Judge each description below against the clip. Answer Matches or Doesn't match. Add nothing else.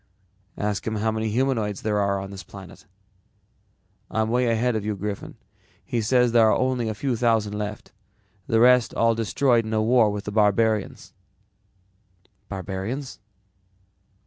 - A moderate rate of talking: Matches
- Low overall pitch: Matches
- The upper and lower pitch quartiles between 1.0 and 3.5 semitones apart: Matches